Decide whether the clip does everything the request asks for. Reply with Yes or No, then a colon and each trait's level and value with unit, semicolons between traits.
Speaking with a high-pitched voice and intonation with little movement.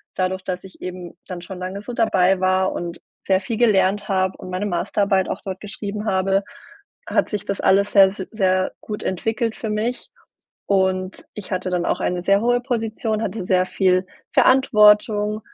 Yes: high, 195 Hz; narrow, 2.2 semitones